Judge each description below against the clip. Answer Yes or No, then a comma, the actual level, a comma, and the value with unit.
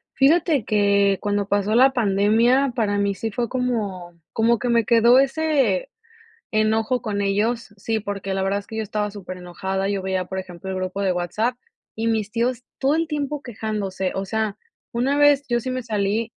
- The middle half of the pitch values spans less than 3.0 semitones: No, average, 3.7 semitones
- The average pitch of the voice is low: No, high, 215 Hz